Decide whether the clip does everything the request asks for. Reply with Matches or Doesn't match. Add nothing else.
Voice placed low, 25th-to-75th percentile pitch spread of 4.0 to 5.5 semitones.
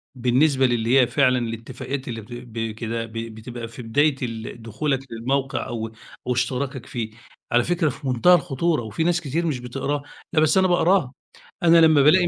Matches